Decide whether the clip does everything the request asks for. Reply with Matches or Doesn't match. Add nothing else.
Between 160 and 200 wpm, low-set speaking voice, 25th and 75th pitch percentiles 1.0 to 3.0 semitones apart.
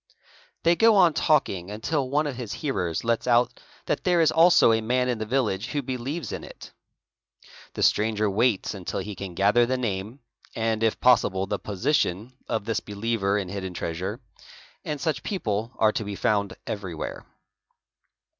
Doesn't match